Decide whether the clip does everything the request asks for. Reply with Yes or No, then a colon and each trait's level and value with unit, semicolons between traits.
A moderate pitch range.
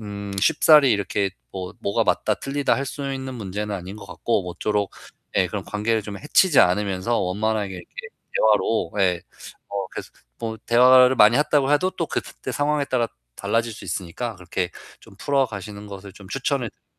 Yes: average, 5.0 semitones